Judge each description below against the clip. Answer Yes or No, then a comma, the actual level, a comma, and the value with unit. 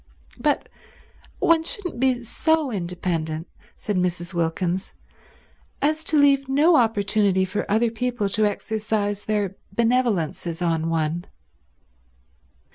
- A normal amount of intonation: No, wide, 5.9 semitones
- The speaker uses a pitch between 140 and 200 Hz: No, high, 210 Hz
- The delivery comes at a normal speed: No, slow, 110 wpm